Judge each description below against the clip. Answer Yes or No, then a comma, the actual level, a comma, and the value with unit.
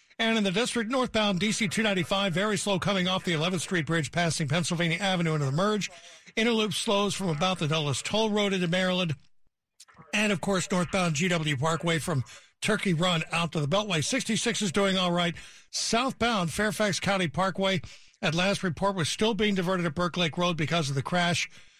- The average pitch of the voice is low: No, medium, 185 Hz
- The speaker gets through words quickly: No, average, 185 wpm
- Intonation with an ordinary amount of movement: Yes, average, 3.3 semitones